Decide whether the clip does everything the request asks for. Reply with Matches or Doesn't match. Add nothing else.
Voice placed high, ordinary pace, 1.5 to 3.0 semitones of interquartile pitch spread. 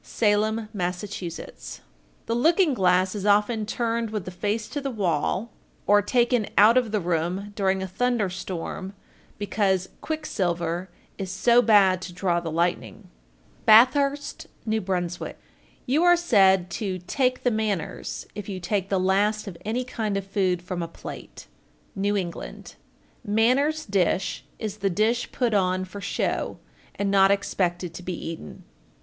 Doesn't match